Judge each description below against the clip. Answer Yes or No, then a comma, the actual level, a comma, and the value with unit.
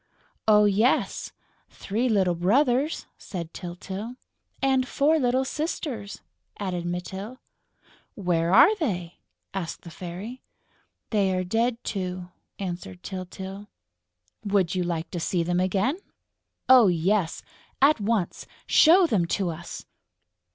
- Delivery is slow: Yes, slow, 115 wpm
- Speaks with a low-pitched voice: No, high, 195 Hz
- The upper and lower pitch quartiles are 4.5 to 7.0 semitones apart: Yes, wide, 5.4 semitones